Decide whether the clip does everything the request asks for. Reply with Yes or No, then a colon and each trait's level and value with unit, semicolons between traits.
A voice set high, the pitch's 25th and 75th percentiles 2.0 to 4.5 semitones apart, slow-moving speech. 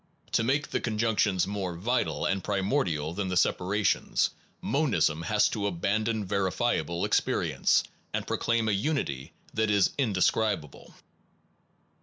No: low, 100 Hz; average, 3.7 semitones; slow, 120 wpm